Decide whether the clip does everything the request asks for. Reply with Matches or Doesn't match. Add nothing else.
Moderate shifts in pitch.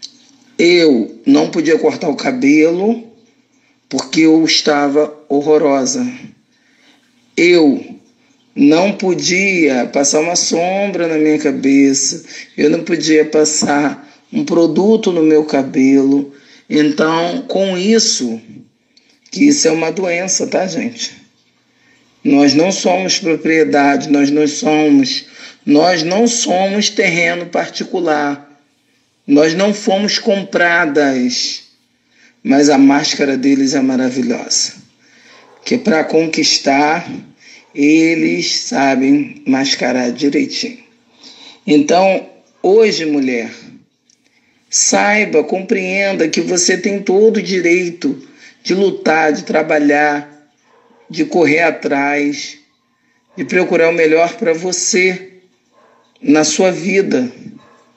Doesn't match